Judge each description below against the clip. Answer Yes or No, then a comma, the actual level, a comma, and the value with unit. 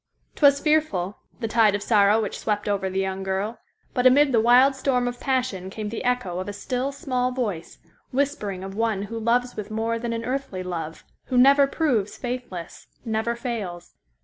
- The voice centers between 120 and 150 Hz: No, high, 230 Hz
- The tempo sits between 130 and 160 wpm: No, average, 175 wpm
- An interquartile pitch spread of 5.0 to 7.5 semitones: No, average, 4.1 semitones